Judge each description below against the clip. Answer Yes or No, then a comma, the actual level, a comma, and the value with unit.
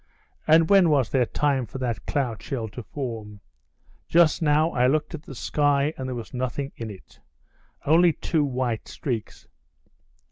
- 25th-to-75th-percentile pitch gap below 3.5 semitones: No, average, 4.1 semitones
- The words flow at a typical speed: Yes, average, 155 wpm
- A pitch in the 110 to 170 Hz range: Yes, low, 135 Hz